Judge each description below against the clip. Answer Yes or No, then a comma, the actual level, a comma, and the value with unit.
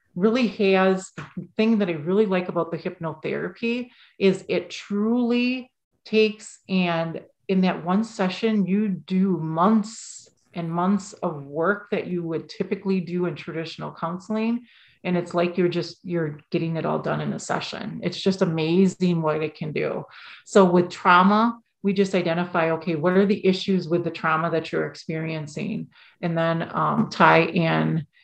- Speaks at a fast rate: No, average, 160 wpm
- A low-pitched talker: No, medium, 180 Hz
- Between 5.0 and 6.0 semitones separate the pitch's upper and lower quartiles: No, average, 3.5 semitones